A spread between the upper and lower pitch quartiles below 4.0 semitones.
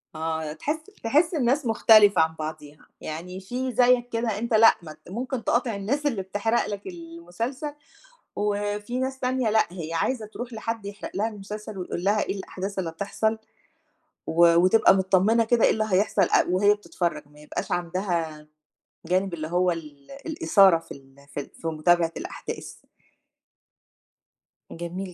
No: average, 5.1 semitones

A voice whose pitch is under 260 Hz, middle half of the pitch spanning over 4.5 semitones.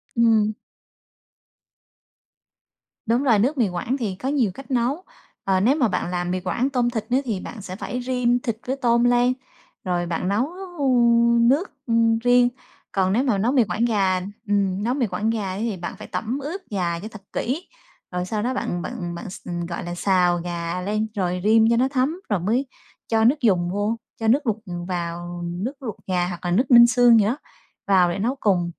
Yes: high, 220 Hz; average, 4.9 semitones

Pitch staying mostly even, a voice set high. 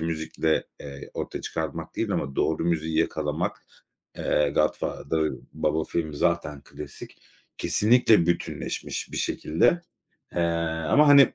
No: narrow, 2.1 semitones; very low, 80 Hz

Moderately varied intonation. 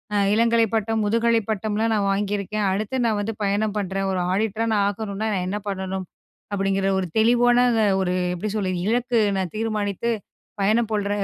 No: narrow, 2.3 semitones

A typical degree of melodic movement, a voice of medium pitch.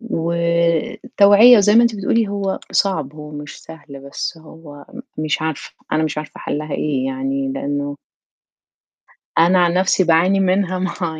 Yes: average, 4.5 semitones; medium, 165 Hz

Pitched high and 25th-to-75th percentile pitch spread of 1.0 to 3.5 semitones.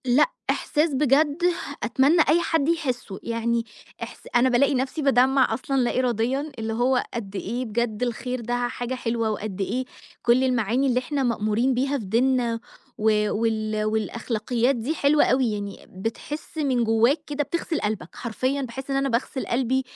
Yes: high, 245 Hz; average, 3.2 semitones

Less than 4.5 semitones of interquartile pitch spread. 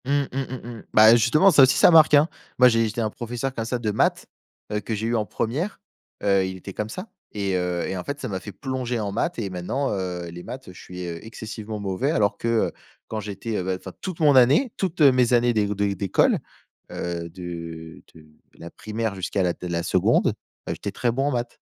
No: average, 5.2 semitones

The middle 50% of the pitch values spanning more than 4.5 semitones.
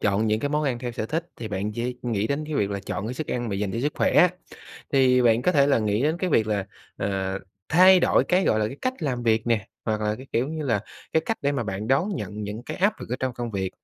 Yes: average, 5.1 semitones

